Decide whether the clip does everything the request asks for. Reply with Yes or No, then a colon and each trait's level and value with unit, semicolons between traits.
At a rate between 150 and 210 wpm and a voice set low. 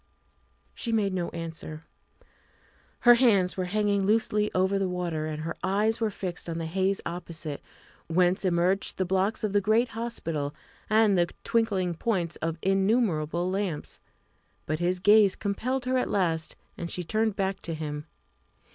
No: average, 155 wpm; high, 190 Hz